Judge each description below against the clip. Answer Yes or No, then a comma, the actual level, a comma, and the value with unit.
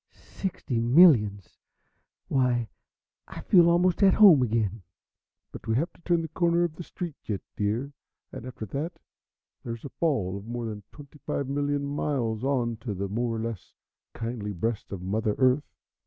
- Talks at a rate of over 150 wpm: Yes, average, 170 wpm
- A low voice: Yes, low, 125 Hz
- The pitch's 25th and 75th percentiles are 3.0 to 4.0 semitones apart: No, average, 5.3 semitones